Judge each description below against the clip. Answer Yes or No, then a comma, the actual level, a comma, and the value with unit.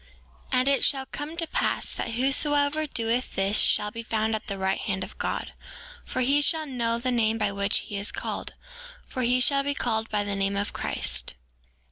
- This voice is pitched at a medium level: No, high, 235 Hz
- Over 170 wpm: Yes, fast, 205 wpm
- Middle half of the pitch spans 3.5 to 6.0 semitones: Yes, average, 5.0 semitones